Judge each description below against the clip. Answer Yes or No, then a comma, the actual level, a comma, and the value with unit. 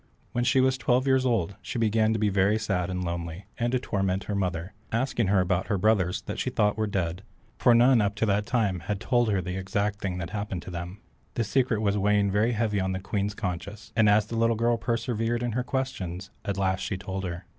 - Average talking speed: No, fast, 230 wpm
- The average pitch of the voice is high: No, low, 105 Hz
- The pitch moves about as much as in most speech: Yes, average, 3.4 semitones